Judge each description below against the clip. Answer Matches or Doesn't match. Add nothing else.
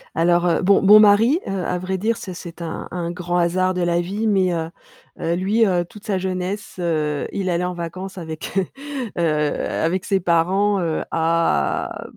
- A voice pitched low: Doesn't match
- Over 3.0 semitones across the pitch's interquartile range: Doesn't match